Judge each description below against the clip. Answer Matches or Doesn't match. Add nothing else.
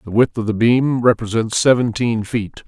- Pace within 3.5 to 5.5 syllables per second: Matches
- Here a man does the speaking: Matches